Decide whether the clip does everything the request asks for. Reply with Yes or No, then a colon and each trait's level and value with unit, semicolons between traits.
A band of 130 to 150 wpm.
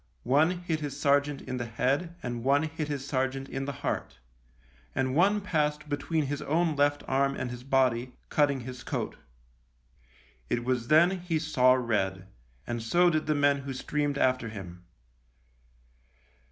No: average, 160 wpm